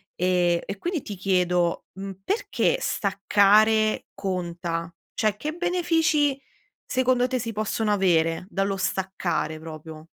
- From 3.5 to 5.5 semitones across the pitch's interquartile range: Yes, average, 5.1 semitones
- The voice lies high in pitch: Yes, high, 195 Hz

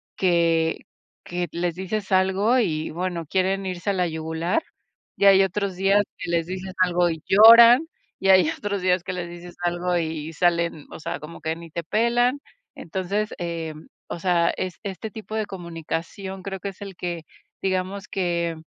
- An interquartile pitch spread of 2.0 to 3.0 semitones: Yes, narrow, 2.4 semitones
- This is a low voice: No, medium, 180 Hz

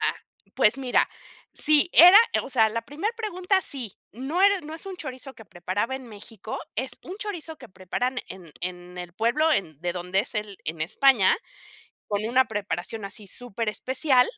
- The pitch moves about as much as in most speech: No, wide, 7.1 semitones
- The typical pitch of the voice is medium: No, high, 235 Hz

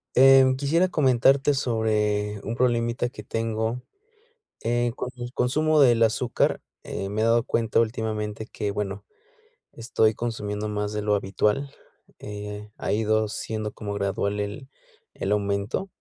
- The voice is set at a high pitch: No, low, 110 Hz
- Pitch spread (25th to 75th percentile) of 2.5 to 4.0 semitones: Yes, average, 2.8 semitones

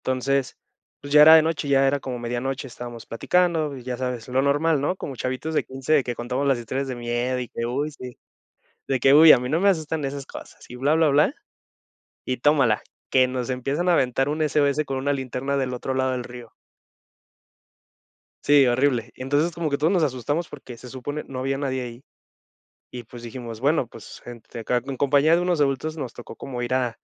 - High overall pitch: No, low, 135 Hz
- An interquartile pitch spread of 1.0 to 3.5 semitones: Yes, average, 2.9 semitones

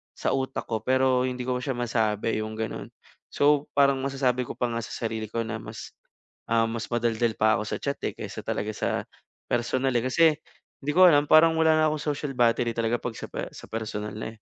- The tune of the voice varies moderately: Yes, average, 3.3 semitones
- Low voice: Yes, low, 120 Hz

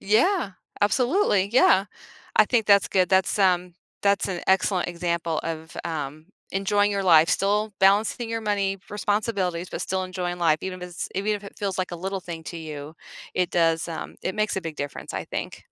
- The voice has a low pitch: No, high, 190 Hz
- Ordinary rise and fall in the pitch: Yes, average, 3.1 semitones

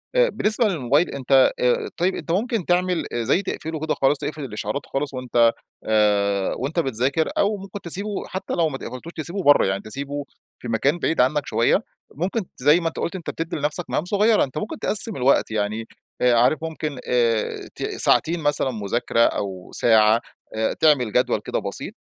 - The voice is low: No, medium, 145 Hz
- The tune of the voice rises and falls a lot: Yes, wide, 6.4 semitones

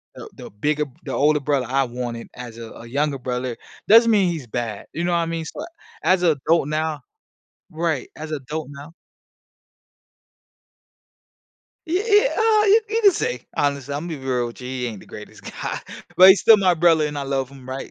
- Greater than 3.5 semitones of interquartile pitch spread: Yes, average, 5.0 semitones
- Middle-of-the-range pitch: Yes, medium, 150 Hz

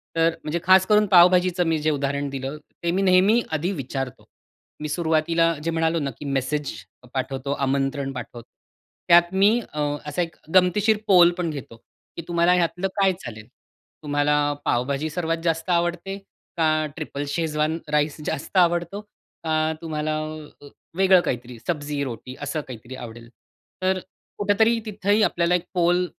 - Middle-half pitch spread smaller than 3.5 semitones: No, average, 4.1 semitones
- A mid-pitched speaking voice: Yes, medium, 160 Hz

